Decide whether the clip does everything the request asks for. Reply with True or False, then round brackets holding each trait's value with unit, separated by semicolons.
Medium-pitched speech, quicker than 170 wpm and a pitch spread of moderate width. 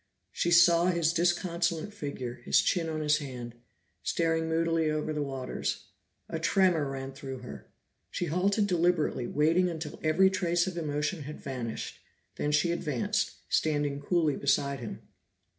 False (160 Hz; 145 wpm; 3.2 semitones)